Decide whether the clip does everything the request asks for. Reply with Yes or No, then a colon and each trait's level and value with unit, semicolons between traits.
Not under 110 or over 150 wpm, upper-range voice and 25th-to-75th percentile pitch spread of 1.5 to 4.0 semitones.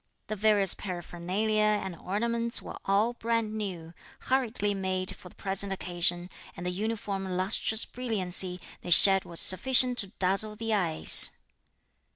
Yes: average, 140 wpm; high, 200 Hz; average, 3.0 semitones